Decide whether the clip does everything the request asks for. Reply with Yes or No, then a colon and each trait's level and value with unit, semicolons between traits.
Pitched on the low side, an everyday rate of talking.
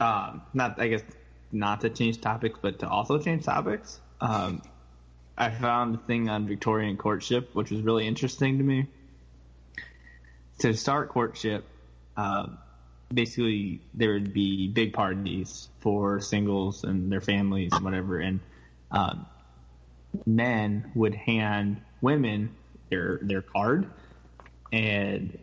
No: low, 100 Hz; slow, 125 wpm